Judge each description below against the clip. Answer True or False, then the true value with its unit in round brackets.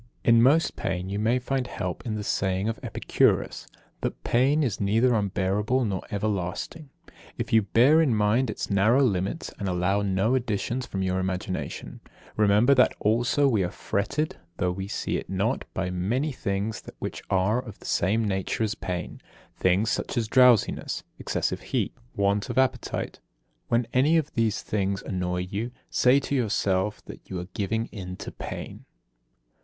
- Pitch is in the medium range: False (105 Hz)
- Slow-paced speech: False (165 wpm)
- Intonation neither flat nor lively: True (4.2 semitones)